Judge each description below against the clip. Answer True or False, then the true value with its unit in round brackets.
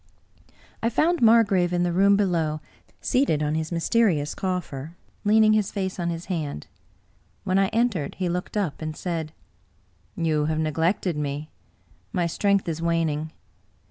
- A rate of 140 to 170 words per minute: True (150 wpm)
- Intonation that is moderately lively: True (4.3 semitones)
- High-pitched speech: False (170 Hz)